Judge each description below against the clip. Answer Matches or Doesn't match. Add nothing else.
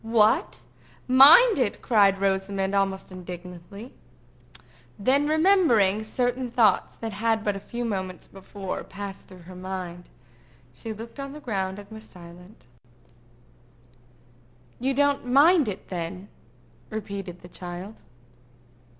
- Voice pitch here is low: Doesn't match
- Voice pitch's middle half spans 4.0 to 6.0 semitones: Matches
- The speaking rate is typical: Doesn't match